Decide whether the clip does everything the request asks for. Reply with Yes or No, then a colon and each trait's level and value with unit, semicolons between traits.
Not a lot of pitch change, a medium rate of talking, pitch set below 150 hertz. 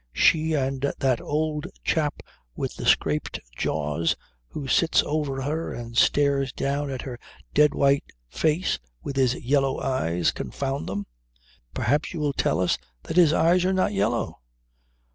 No: average, 3.4 semitones; average, 150 wpm; medium, 140 Hz